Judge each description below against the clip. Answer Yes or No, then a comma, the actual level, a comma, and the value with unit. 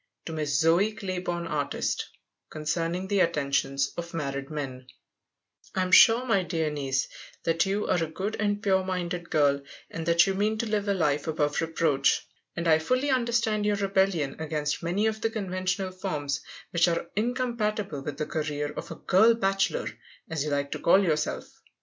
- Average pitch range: Yes, average, 5.0 semitones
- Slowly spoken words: No, average, 175 wpm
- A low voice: No, medium, 175 Hz